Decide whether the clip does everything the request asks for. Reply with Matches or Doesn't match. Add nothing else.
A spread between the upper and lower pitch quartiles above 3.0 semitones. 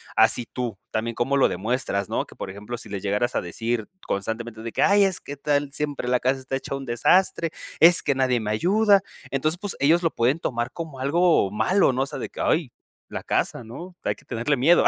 Matches